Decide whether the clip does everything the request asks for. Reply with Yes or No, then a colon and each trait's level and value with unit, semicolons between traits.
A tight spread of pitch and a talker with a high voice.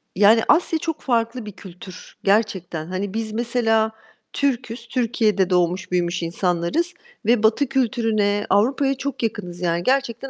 No: average, 4.7 semitones; high, 220 Hz